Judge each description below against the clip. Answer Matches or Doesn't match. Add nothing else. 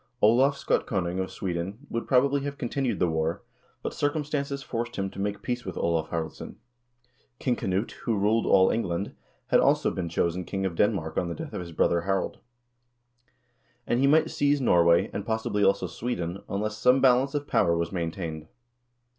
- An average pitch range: Doesn't match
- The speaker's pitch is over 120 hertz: Doesn't match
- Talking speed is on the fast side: Doesn't match